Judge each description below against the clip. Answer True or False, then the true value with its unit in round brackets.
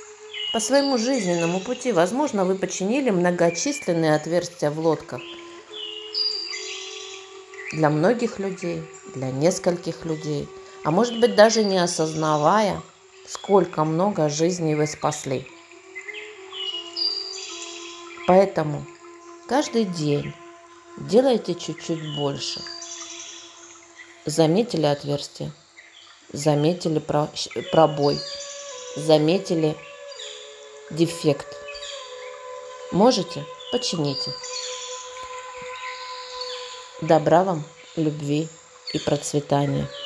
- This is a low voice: False (195 Hz)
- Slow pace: True (70 wpm)